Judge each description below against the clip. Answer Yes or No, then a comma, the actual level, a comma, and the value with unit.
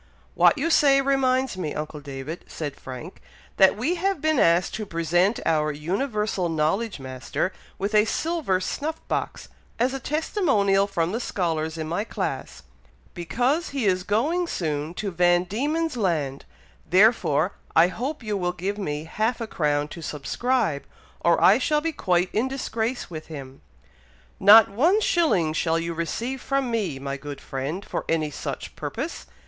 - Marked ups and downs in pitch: Yes, wide, 8.0 semitones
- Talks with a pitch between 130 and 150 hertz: No, high, 195 Hz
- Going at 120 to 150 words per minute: No, average, 160 wpm